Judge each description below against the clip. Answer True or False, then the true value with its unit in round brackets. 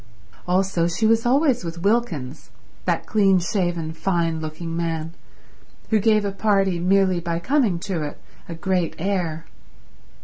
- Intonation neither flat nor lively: True (3.4 semitones)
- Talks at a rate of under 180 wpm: True (140 wpm)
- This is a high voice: False (180 Hz)